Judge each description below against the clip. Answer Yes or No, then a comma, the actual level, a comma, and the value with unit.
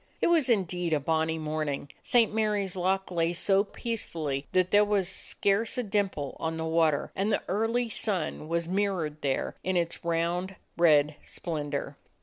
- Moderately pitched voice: Yes, medium, 175 Hz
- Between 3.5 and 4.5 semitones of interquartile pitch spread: Yes, average, 4.1 semitones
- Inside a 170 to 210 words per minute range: No, average, 160 wpm